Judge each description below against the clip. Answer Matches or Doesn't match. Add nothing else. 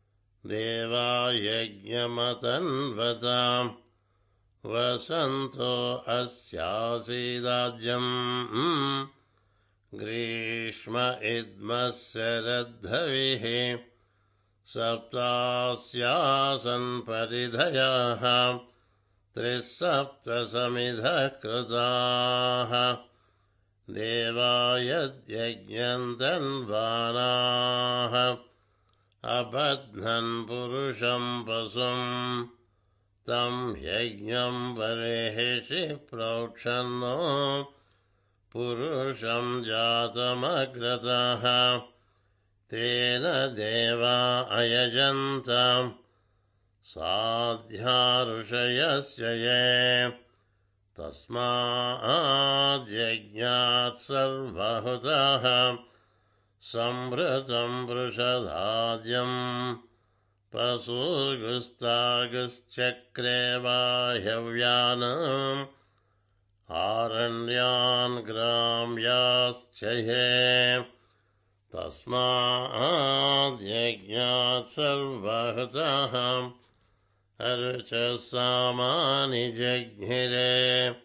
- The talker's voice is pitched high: Doesn't match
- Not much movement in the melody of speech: Matches